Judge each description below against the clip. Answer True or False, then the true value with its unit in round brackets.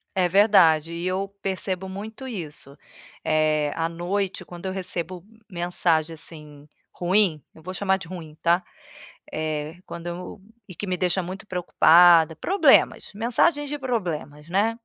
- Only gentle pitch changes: False (3.2 semitones)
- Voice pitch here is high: False (180 Hz)